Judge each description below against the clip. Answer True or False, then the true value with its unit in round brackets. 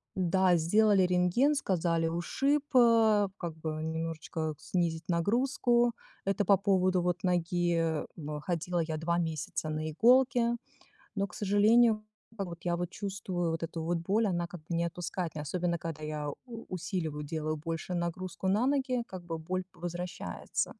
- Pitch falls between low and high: True (175 Hz)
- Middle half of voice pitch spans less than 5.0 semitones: True (3.5 semitones)